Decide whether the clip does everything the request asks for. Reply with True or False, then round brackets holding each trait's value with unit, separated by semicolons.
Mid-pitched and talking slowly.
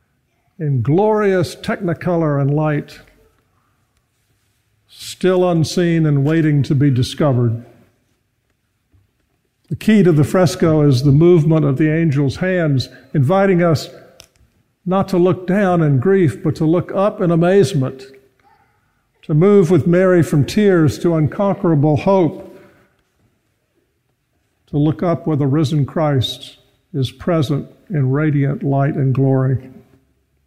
True (150 Hz; 120 wpm)